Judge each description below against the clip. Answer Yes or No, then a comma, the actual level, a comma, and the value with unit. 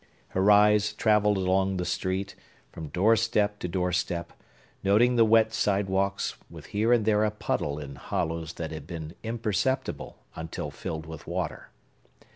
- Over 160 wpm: No, average, 145 wpm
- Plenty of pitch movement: No, average, 3.8 semitones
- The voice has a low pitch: Yes, very low, 95 Hz